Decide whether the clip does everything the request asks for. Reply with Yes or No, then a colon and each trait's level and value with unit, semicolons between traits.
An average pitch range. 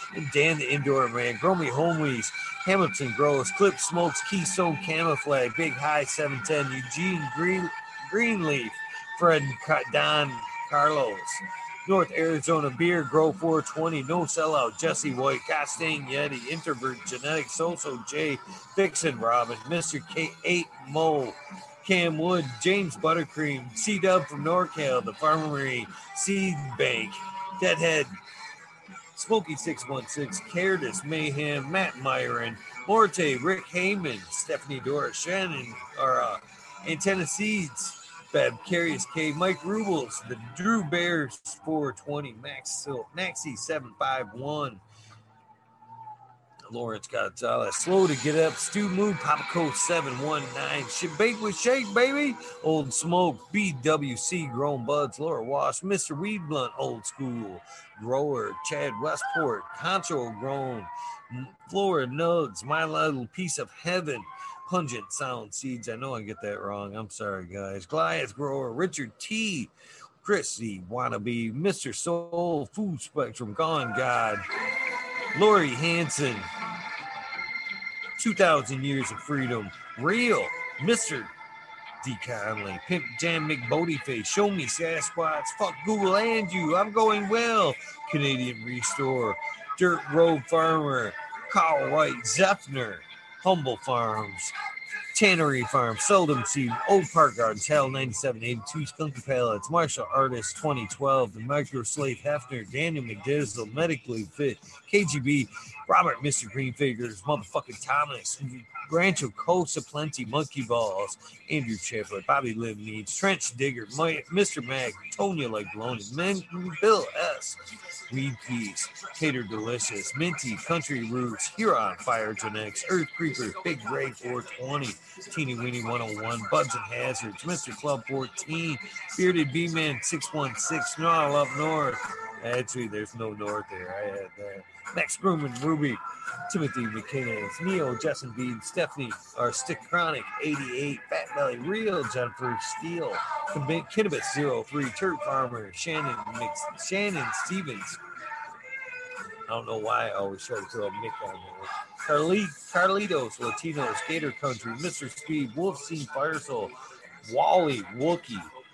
No: wide, 6.5 semitones